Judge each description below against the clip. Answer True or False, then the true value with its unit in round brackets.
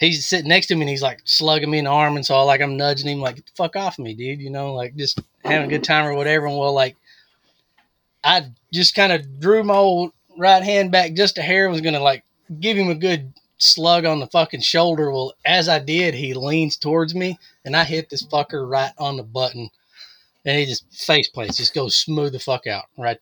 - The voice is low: False (150 Hz)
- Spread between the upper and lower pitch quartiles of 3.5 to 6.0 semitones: True (3.8 semitones)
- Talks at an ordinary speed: False (245 wpm)